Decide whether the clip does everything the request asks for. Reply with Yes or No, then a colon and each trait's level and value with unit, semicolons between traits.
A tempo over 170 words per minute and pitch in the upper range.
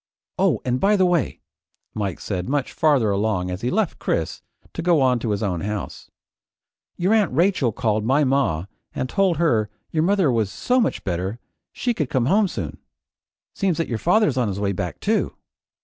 No: average, 190 wpm; low, 130 Hz